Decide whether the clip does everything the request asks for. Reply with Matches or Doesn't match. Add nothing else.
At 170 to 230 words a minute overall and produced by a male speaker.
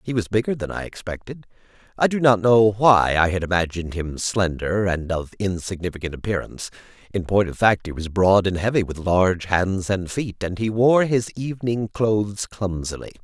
Matches